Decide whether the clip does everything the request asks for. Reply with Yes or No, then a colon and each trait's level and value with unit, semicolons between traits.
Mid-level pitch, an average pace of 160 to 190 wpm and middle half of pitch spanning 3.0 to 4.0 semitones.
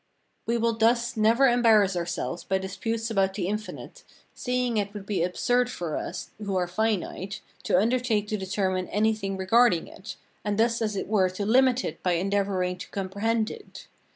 No: high, 210 Hz; average, 175 wpm; average, 3.3 semitones